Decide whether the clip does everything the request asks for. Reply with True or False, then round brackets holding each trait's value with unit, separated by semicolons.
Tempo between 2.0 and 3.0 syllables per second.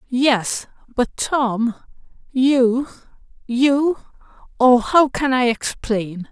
True (2.6 syllables/s)